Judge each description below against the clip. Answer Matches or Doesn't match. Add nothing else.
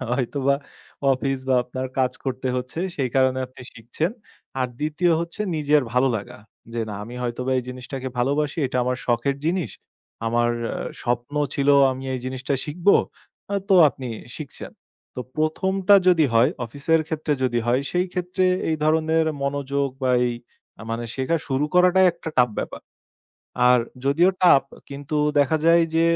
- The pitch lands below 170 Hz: Matches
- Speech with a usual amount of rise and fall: Matches